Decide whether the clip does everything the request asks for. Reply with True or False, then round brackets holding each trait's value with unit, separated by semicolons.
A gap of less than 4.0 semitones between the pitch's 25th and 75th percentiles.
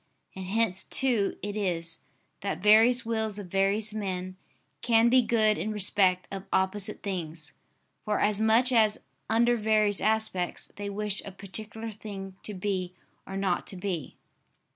True (2.5 semitones)